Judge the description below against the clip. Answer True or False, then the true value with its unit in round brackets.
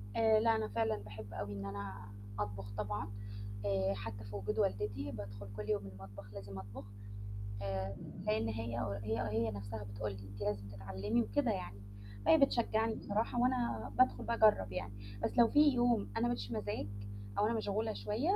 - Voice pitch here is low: True (105 Hz)